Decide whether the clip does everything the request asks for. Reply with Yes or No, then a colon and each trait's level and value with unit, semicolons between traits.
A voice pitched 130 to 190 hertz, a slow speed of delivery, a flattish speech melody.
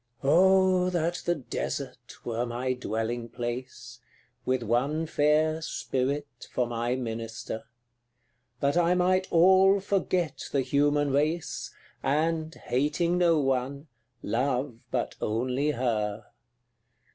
No: medium, 140 Hz; slow, 110 wpm; average, 5.2 semitones